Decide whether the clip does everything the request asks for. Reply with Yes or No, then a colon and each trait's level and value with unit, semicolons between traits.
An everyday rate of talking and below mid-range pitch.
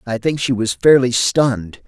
Yes: average, 190 wpm; low, 125 Hz